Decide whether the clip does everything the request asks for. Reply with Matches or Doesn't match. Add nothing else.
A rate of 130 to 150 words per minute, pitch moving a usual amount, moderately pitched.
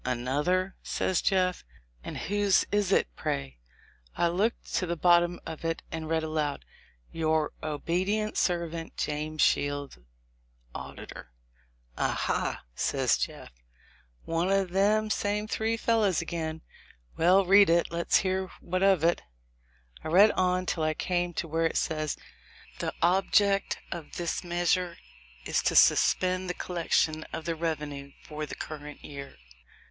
Matches